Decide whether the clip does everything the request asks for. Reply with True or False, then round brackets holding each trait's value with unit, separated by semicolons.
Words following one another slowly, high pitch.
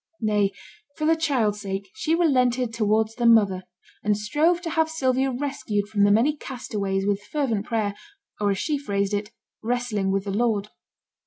False (170 wpm; 220 Hz)